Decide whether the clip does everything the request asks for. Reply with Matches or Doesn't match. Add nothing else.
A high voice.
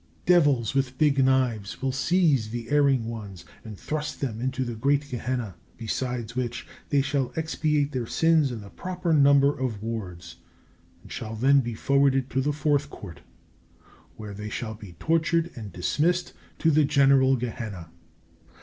Doesn't match